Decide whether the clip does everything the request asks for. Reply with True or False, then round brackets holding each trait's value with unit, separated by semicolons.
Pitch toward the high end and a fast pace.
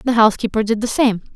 True (220 Hz; 220 wpm)